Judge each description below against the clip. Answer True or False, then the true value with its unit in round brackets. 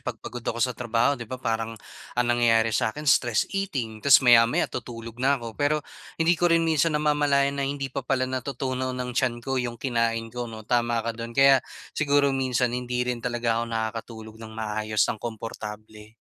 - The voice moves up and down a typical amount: True (3.1 semitones)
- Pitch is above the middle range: False (120 Hz)